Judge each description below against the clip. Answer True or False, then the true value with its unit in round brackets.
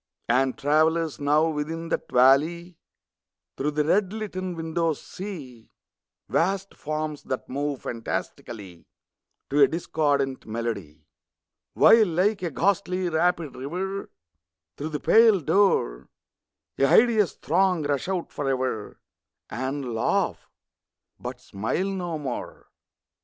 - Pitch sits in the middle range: True (155 Hz)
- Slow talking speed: True (110 wpm)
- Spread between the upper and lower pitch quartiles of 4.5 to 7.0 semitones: True (5.2 semitones)